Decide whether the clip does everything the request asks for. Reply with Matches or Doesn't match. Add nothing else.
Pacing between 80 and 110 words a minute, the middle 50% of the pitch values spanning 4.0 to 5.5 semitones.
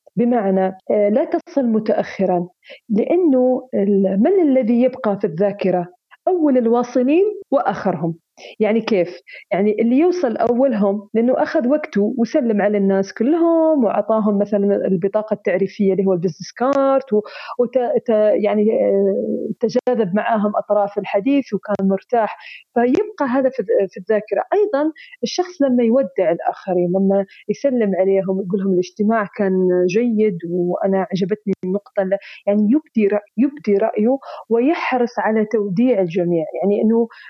Doesn't match